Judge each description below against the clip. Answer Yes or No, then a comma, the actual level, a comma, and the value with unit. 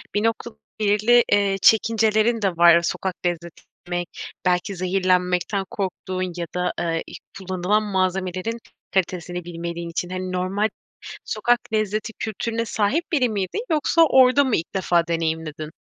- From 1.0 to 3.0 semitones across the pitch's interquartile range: No, average, 3.6 semitones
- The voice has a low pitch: No, high, 190 Hz